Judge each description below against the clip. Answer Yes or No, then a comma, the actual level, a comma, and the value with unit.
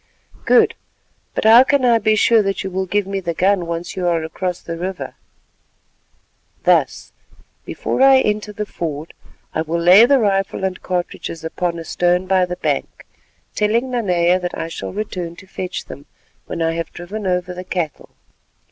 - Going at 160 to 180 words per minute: Yes, average, 175 wpm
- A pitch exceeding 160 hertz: Yes, medium, 185 Hz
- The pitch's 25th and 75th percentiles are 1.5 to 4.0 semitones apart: Yes, average, 3.3 semitones